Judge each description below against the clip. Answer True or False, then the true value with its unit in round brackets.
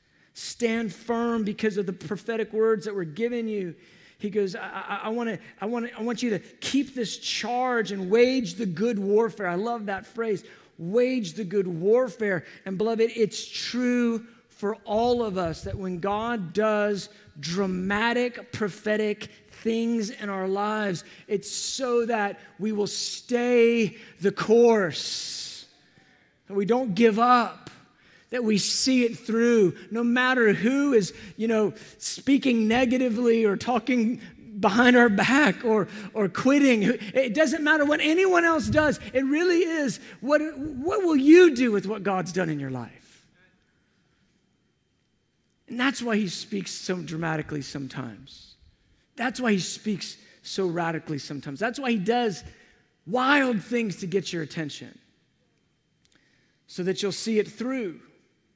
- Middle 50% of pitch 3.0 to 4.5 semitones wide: True (3.6 semitones)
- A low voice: False (220 Hz)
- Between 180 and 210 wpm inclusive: False (150 wpm)